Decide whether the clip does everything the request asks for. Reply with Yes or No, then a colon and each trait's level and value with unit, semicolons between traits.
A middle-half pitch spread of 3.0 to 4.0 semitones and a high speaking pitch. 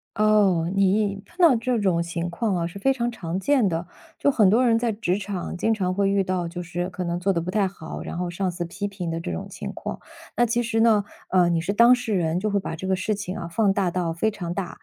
Yes: average, 3.5 semitones; high, 195 Hz